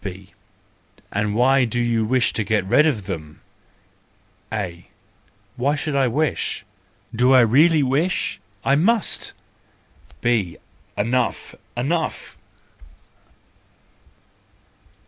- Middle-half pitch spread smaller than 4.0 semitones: No, average, 4.9 semitones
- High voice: No, low, 120 Hz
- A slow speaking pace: Yes, slow, 90 wpm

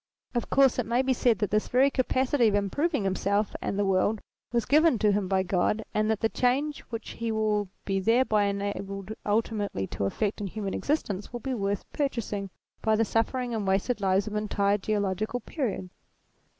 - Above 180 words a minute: Yes, average, 190 wpm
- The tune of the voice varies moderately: Yes, average, 3.4 semitones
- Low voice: No, high, 215 Hz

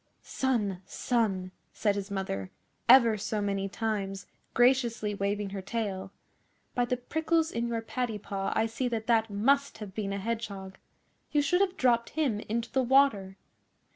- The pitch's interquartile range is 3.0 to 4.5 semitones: Yes, average, 3.8 semitones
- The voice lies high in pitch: Yes, high, 220 Hz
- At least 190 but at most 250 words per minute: No, average, 160 wpm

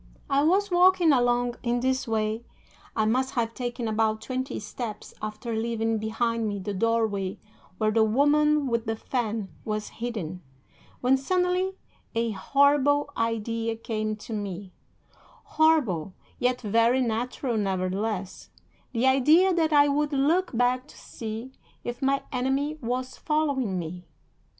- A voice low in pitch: No, high, 235 Hz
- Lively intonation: No, average, 4.1 semitones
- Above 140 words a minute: No, slow, 135 wpm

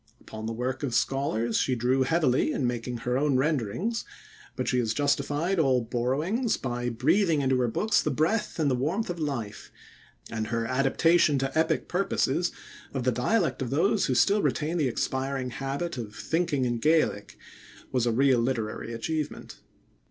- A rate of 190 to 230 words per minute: No, average, 170 wpm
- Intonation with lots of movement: No, average, 4.6 semitones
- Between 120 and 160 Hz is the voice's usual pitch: Yes, low, 135 Hz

